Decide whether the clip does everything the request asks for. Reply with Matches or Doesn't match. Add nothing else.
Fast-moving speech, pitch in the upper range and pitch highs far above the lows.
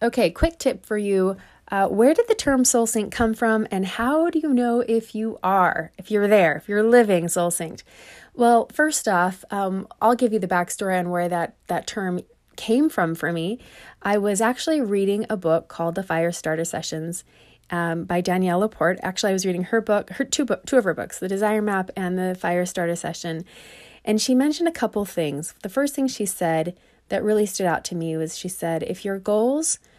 Doesn't match